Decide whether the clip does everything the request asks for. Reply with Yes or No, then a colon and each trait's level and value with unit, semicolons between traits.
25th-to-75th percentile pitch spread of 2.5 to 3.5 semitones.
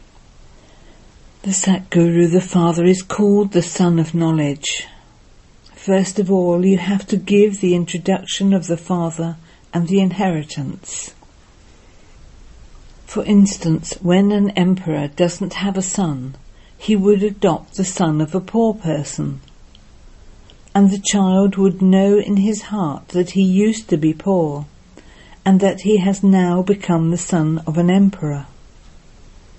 Yes: average, 3.1 semitones